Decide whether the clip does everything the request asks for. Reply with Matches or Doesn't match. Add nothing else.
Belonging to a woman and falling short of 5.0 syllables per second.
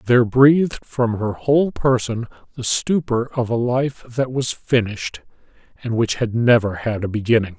Doesn't match